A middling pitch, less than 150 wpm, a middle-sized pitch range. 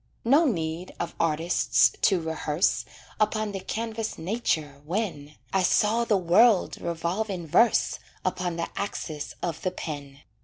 Yes: medium, 180 Hz; average, 140 wpm; average, 4.9 semitones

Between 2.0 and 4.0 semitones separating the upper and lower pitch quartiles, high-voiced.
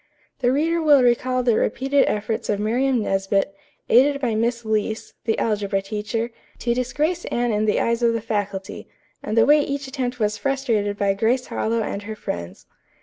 Yes: average, 3.6 semitones; high, 230 Hz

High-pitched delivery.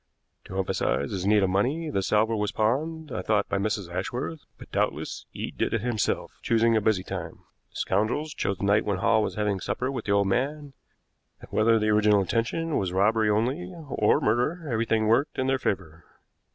No: low, 110 Hz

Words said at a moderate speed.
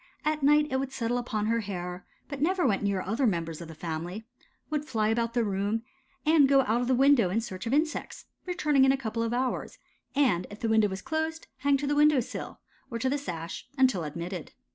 No: fast, 225 wpm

